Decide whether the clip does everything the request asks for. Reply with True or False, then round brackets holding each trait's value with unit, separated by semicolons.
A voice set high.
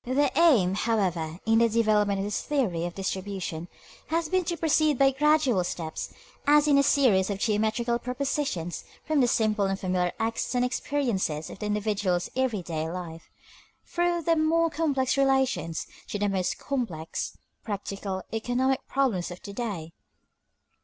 True (220 Hz)